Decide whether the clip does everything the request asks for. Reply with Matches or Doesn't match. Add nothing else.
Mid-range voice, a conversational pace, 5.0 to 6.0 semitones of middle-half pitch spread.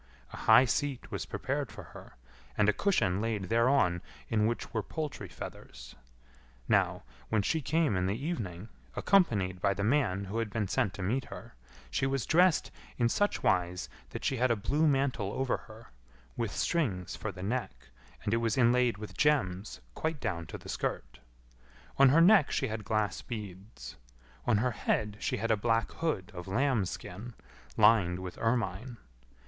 Doesn't match